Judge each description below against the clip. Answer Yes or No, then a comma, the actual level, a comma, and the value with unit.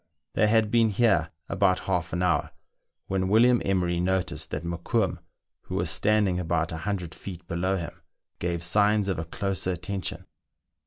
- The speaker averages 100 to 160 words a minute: Yes, average, 155 wpm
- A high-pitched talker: No, very low, 95 Hz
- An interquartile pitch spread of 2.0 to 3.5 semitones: Yes, average, 2.8 semitones